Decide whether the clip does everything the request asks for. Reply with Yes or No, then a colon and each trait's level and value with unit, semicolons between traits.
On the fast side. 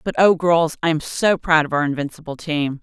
Yes: fast, 235 wpm